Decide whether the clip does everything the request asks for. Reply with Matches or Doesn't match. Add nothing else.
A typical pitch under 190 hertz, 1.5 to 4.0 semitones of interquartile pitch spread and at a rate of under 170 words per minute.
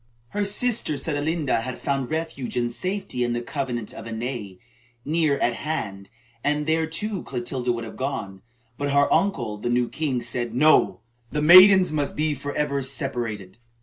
Doesn't match